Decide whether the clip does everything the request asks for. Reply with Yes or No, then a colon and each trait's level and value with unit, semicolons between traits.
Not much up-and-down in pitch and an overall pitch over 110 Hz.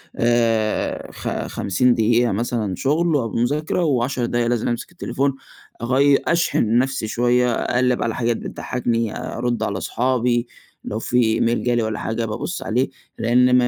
Yes: narrow, 1.7 semitones; low, 120 Hz